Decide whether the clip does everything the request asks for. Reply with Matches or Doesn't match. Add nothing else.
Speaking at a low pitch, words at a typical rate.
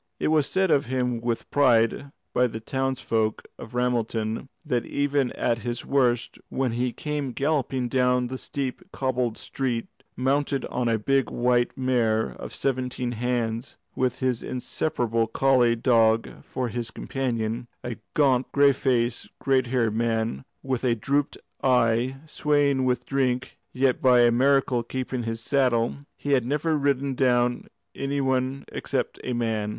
Matches